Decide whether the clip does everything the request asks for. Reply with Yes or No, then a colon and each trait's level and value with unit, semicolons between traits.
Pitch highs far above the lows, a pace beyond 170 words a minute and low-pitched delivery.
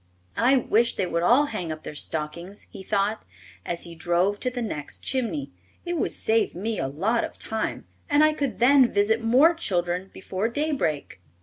No: wide, 6.2 semitones; average, 185 wpm; high, 210 Hz